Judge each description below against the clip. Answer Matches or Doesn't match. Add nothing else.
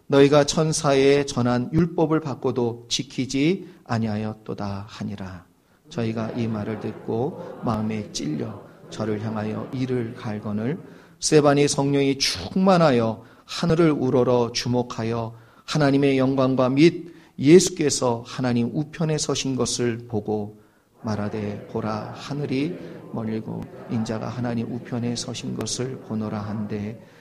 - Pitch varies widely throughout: Doesn't match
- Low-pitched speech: Matches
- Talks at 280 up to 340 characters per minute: Doesn't match